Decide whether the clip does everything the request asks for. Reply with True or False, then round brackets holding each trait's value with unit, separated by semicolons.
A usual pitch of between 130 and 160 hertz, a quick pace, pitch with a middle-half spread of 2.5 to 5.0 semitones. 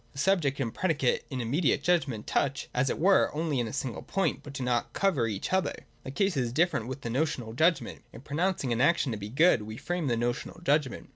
False (140 Hz; 230 wpm; 5.6 semitones)